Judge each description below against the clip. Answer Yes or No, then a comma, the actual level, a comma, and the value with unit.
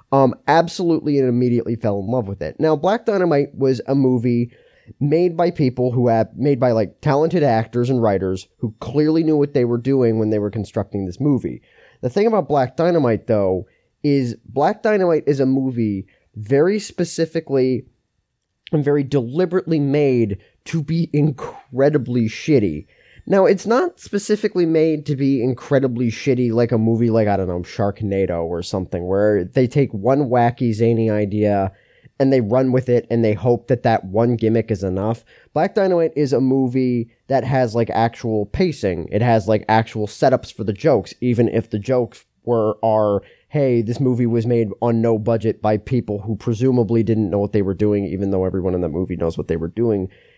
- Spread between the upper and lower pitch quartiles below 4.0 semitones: No, average, 4.5 semitones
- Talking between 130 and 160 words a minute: No, average, 185 wpm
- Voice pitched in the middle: No, low, 120 Hz